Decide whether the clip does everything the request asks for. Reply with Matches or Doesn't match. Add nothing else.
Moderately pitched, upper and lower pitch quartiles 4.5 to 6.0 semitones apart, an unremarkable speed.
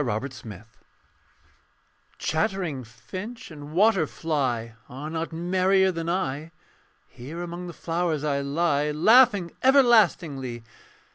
Doesn't match